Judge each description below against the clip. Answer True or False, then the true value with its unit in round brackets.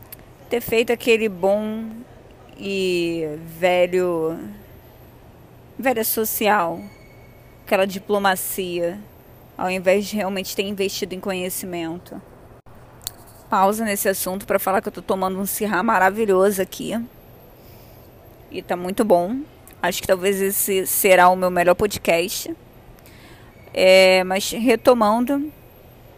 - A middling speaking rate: False (110 wpm)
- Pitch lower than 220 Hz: True (190 Hz)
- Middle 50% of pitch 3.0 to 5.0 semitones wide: True (4.1 semitones)